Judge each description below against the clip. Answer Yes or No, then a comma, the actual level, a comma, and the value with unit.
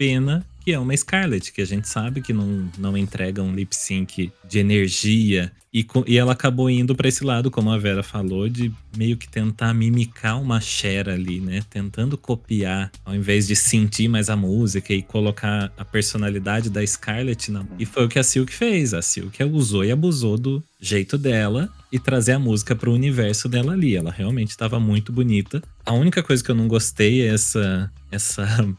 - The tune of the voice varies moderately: Yes, average, 4.0 semitones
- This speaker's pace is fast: Yes, fast, 200 wpm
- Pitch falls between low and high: No, low, 110 Hz